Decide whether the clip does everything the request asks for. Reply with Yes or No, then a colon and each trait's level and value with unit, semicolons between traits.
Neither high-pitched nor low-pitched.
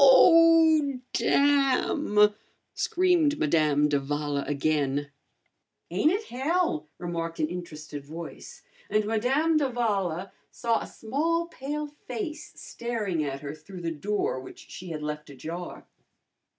No: high, 200 Hz